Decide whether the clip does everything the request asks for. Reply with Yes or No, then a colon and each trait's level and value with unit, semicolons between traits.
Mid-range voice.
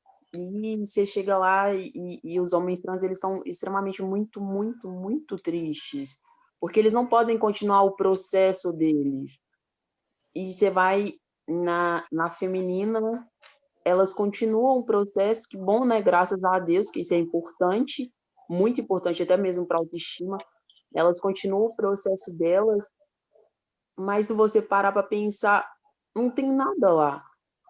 No: high, 195 Hz